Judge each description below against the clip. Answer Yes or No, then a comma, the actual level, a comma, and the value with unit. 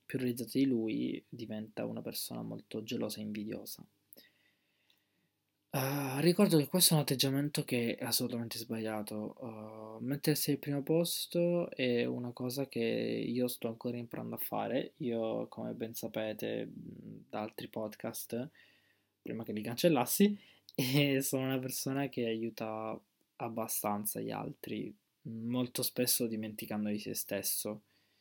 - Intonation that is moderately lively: Yes, average, 3.9 semitones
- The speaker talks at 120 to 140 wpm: Yes, average, 135 wpm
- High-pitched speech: No, low, 120 Hz